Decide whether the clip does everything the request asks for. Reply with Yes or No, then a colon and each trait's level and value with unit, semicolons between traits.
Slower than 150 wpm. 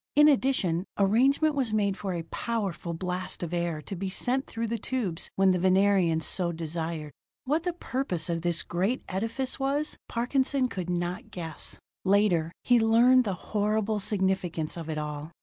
No: average, 165 wpm